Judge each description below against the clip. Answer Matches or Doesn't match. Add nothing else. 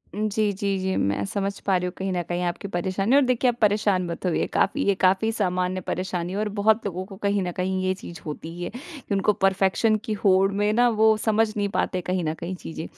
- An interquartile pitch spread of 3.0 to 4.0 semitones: Doesn't match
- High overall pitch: Matches